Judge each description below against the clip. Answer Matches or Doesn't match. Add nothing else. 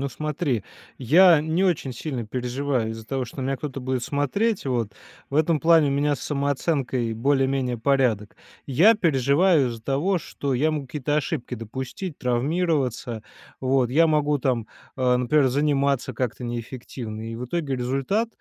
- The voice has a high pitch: Doesn't match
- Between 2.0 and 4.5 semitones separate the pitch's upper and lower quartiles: Matches